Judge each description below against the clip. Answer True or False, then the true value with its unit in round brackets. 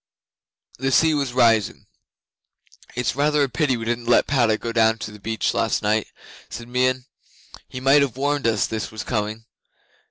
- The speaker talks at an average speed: True (170 wpm)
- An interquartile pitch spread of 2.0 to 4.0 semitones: True (3.2 semitones)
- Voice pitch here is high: False (120 Hz)